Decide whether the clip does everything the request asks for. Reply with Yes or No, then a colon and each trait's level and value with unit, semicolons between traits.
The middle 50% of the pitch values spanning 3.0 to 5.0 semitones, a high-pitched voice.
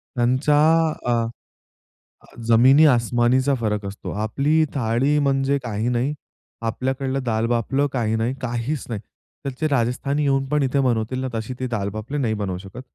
No: average, 3.3 semitones; low, 125 Hz